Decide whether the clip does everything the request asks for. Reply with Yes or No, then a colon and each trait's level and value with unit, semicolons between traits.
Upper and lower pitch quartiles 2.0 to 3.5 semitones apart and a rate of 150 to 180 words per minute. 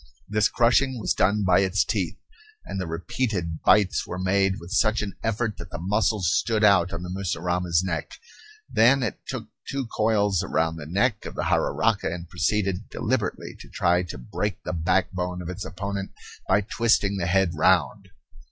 Yes: average, 3.0 semitones; average, 170 wpm